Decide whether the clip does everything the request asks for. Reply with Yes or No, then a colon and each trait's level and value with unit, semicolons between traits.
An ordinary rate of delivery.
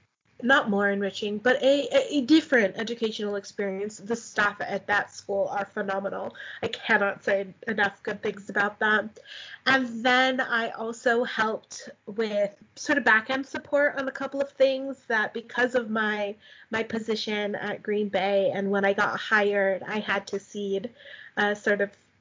Yes: average, 170 wpm